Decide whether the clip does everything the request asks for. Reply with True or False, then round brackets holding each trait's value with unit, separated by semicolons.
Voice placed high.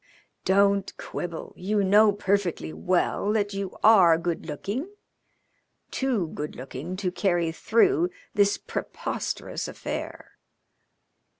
True (195 Hz)